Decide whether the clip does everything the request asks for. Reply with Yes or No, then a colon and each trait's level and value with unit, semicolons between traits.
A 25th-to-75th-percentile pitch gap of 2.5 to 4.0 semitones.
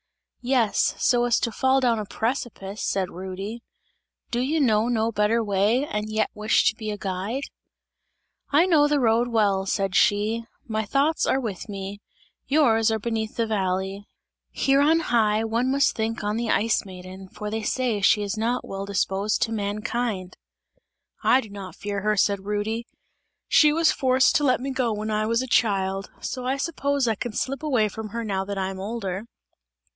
Yes: average, 3.4 semitones